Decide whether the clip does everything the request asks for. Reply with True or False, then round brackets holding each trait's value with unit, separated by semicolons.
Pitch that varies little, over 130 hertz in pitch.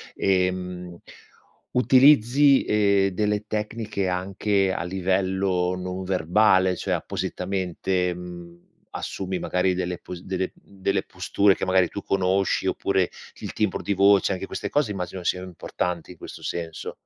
False (1.6 semitones; 95 Hz)